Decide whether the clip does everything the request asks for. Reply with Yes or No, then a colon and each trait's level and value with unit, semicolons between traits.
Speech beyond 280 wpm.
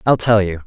No: fast, 270 wpm